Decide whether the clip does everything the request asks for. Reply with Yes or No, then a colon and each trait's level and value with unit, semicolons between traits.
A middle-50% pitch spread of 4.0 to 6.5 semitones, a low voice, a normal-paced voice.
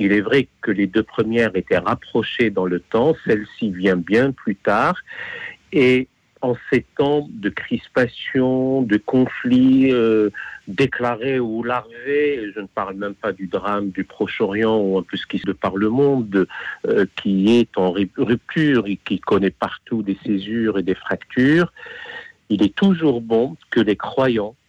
Yes: average, 4.6 semitones; low, 115 Hz; average, 165 wpm